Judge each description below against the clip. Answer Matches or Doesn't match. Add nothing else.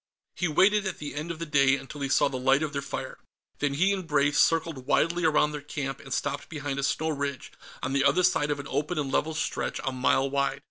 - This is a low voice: Doesn't match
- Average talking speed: Doesn't match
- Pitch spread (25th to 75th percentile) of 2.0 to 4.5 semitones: Matches